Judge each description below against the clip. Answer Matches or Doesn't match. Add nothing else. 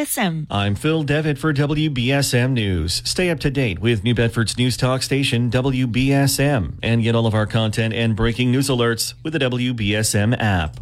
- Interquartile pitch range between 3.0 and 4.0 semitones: Matches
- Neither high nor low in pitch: Doesn't match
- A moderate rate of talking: Matches